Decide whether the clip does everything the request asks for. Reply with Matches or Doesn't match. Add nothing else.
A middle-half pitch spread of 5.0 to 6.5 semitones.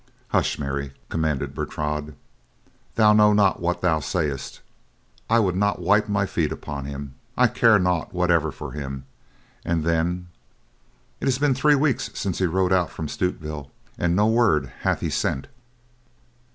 Matches